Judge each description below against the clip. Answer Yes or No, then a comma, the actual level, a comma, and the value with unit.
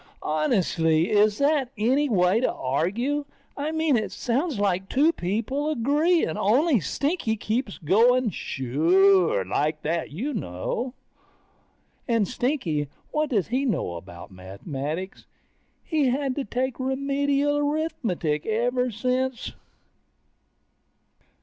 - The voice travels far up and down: Yes, wide, 8.0 semitones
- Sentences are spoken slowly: Yes, slow, 110 wpm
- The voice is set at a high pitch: Yes, high, 230 Hz